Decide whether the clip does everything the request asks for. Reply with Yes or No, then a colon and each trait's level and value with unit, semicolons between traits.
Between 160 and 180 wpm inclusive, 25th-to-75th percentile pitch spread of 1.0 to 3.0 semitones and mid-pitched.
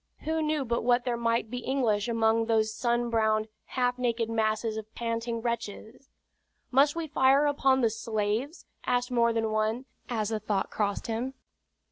No: average, 165 wpm; narrow, 2.4 semitones; high, 235 Hz